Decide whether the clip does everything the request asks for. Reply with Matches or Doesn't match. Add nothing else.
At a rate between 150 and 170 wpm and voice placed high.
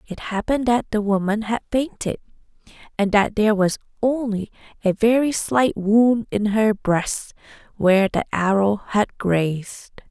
Doesn't match